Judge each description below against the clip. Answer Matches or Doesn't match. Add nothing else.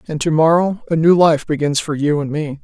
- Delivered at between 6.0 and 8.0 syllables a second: Doesn't match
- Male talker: Doesn't match